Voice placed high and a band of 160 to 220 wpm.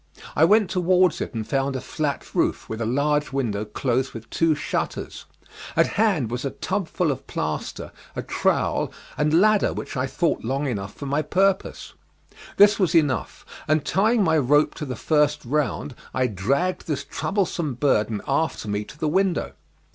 No: medium, 150 Hz; average, 170 wpm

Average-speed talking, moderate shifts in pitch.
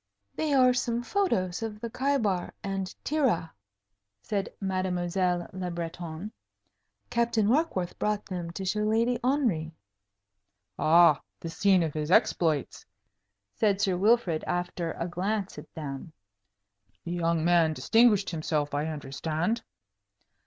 No: slow, 125 wpm; average, 4.7 semitones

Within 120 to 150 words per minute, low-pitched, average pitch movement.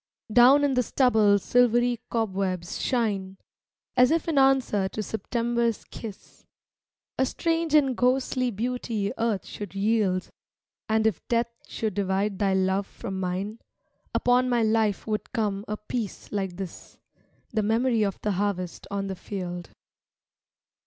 No: average, 140 wpm; high, 215 Hz; average, 3.8 semitones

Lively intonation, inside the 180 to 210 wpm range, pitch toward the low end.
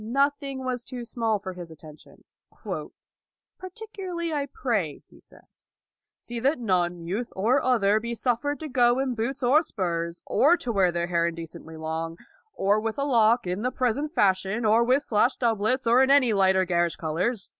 No: wide, 6.0 semitones; average, 185 wpm; high, 230 Hz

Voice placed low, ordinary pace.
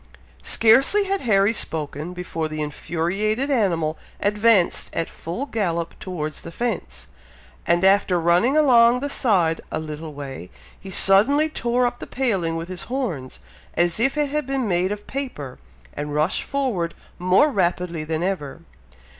No: medium, 185 Hz; average, 150 wpm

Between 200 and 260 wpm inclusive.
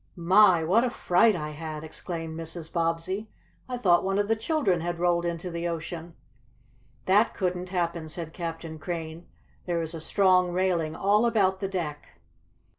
No: average, 165 wpm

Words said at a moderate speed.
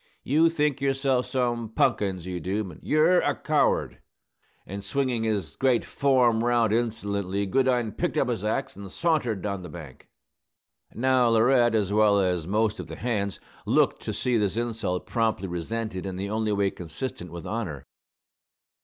Yes: average, 160 wpm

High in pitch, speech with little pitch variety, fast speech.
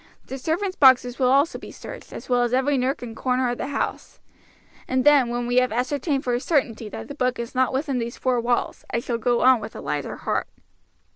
Yes: very high, 255 Hz; narrow, 1.9 semitones; fast, 230 wpm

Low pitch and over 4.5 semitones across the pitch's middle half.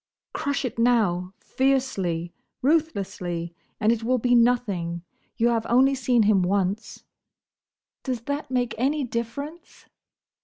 No: high, 235 Hz; average, 5.0 semitones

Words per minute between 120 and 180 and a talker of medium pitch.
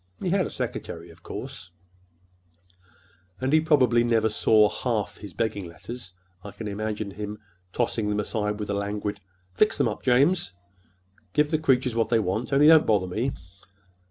No: average, 160 wpm; low, 110 Hz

